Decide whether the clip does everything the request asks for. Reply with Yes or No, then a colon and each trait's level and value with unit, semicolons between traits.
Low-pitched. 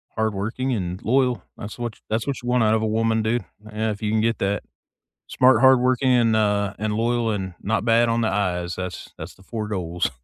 Yes: low, 110 Hz